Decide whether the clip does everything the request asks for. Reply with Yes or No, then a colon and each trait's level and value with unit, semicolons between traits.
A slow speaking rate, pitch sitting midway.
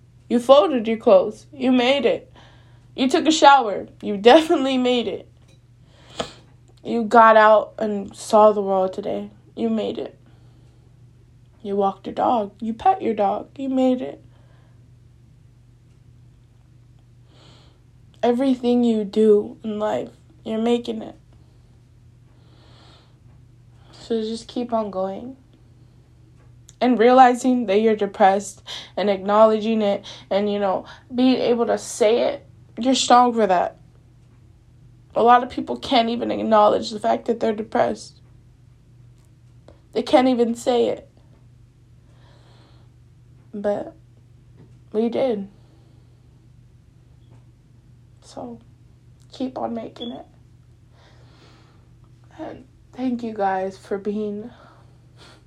No: slow, 110 wpm; low, 125 Hz